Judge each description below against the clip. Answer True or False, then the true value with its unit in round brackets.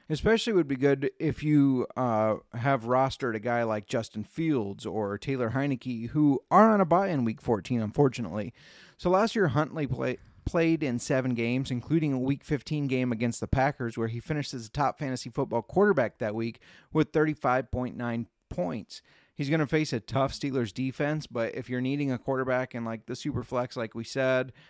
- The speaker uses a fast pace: False (195 wpm)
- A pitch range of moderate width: True (3.9 semitones)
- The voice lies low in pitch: True (130 Hz)